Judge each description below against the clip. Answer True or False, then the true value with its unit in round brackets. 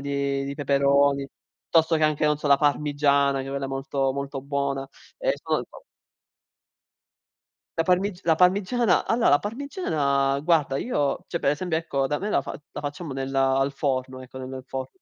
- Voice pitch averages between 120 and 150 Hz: True (140 Hz)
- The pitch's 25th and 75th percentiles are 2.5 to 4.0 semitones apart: True (2.8 semitones)